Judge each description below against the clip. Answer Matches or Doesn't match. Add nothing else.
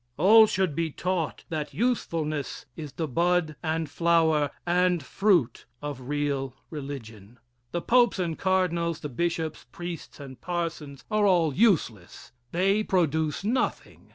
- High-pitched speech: Doesn't match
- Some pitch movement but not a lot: Matches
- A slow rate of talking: Matches